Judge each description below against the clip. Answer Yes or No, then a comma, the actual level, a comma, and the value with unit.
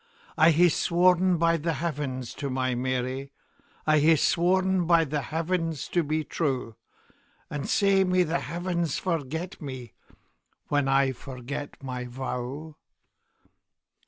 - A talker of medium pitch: Yes, medium, 155 Hz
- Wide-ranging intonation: No, average, 4.4 semitones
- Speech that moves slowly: Yes, slow, 115 wpm